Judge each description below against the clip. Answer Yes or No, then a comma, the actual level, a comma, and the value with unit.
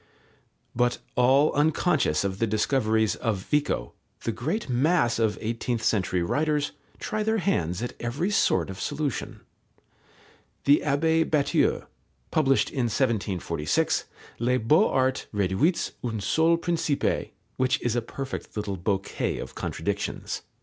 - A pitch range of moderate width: No, wide, 5.7 semitones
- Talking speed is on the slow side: Yes, slow, 130 wpm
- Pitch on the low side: Yes, low, 125 Hz